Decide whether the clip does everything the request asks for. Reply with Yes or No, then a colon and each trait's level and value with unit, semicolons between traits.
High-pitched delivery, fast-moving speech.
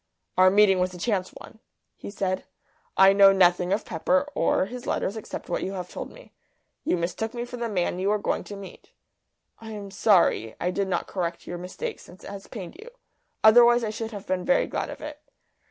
Yes: high, 195 Hz; fast, 215 wpm